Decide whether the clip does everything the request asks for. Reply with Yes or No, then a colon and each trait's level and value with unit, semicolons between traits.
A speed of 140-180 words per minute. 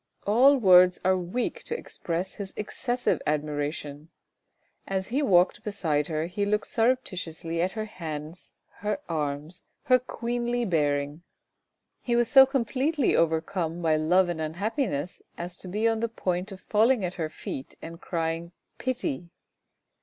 Yes: average, 150 wpm